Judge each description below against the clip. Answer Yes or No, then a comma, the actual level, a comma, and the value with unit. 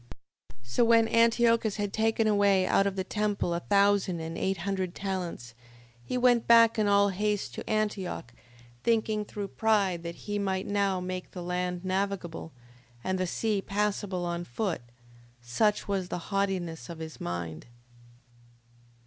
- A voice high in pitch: Yes, high, 195 Hz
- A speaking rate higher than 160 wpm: No, average, 155 wpm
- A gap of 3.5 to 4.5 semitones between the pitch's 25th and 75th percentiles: No, average, 2.8 semitones